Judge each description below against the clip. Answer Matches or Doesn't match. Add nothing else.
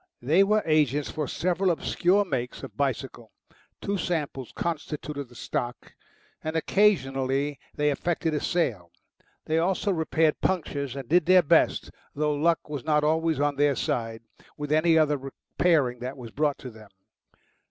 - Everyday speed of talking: Matches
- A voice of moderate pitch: Matches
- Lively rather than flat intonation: Doesn't match